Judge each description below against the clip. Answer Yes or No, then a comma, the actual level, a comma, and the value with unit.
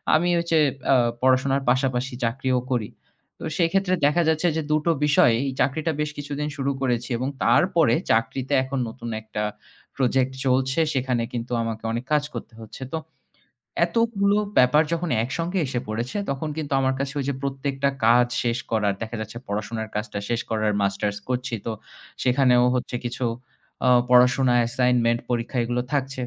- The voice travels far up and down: No, average, 3.3 semitones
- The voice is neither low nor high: No, low, 130 Hz